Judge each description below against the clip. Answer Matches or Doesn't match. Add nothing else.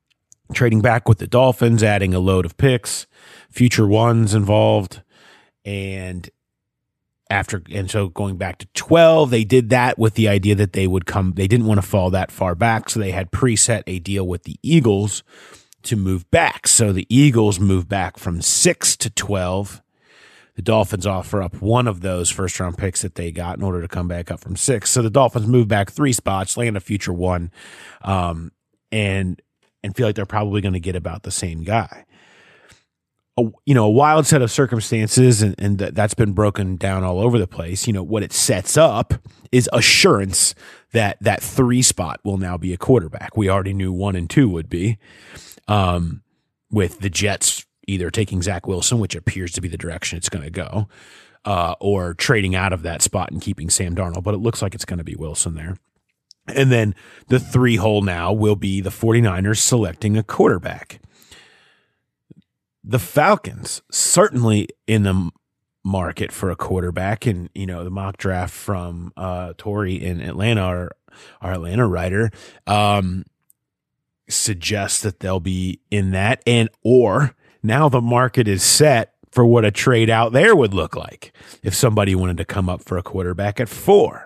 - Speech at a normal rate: Matches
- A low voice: Matches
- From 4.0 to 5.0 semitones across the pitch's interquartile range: Doesn't match